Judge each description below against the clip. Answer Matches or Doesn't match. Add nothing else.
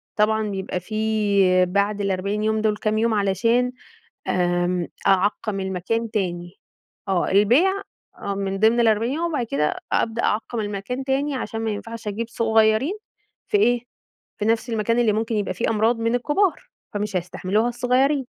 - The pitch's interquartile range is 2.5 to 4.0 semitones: Matches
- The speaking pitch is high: Matches